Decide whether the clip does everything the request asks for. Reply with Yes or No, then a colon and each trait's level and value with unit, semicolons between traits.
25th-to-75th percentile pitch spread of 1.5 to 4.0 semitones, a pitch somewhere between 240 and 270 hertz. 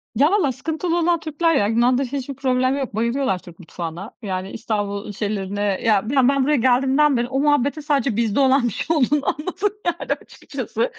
No: average, 5.1 semitones; very high, 260 Hz